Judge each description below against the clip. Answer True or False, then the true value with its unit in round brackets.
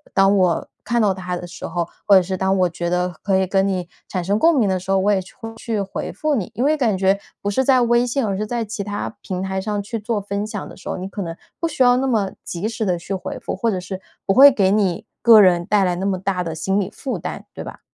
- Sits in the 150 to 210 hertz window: True (195 Hz)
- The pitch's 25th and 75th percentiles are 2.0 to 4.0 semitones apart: True (3.1 semitones)